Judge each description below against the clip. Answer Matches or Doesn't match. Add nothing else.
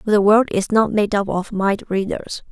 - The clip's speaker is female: Matches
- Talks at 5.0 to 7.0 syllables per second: Doesn't match